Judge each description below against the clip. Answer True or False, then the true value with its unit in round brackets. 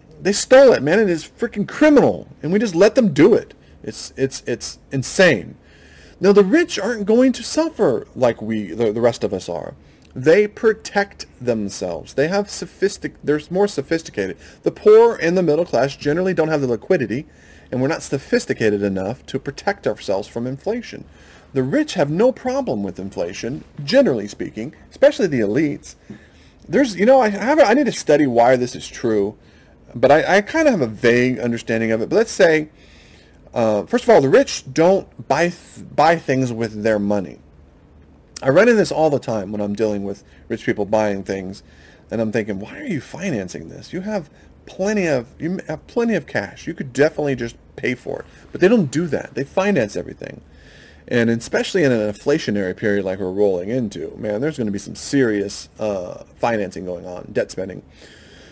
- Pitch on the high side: False (135 Hz)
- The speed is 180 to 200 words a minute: True (190 wpm)